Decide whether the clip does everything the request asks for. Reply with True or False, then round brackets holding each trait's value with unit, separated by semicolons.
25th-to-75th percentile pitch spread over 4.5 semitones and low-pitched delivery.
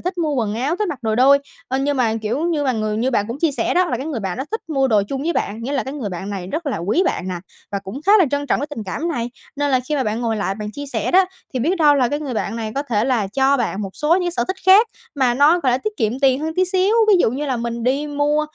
False (5.1 semitones; 270 Hz)